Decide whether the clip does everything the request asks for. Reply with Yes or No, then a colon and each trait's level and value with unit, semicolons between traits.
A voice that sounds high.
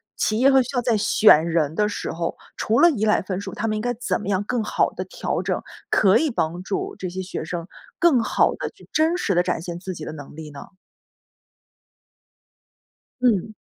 Yes: high, 205 Hz